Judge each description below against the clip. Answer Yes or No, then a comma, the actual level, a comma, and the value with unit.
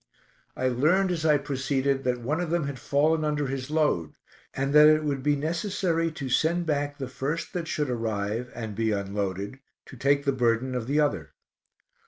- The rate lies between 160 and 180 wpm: No, average, 190 wpm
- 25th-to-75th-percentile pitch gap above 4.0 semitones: No, average, 3.7 semitones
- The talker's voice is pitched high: No, medium, 140 Hz